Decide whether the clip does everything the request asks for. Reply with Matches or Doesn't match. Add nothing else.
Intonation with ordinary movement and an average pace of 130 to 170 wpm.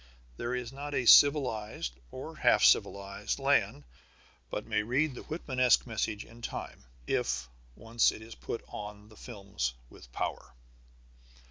Matches